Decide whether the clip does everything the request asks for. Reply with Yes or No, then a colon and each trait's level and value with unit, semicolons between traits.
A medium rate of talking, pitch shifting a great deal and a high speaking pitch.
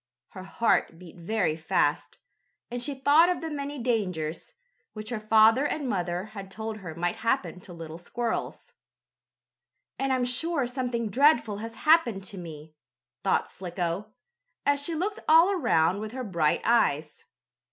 Yes: average, 150 wpm; wide, 7.2 semitones; high, 220 Hz